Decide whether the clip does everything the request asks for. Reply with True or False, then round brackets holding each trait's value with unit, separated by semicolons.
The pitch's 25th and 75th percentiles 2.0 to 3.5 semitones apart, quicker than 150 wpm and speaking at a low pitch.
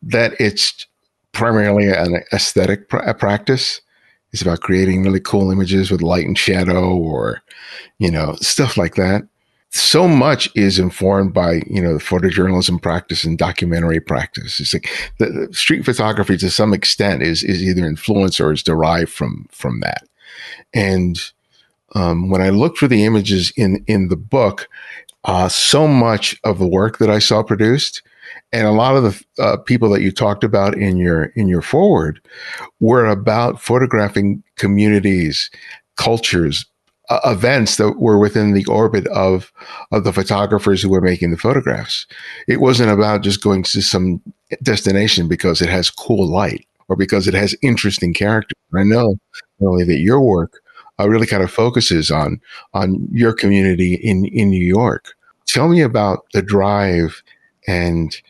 True (2.9 semitones; 165 wpm; 100 Hz)